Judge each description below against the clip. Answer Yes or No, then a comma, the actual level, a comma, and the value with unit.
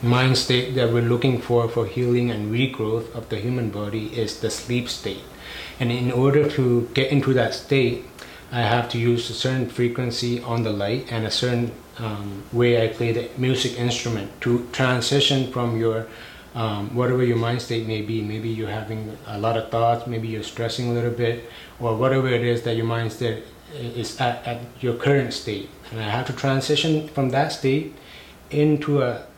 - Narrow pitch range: Yes, narrow, 1.8 semitones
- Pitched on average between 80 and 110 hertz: No, low, 120 Hz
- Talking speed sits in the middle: Yes, average, 190 wpm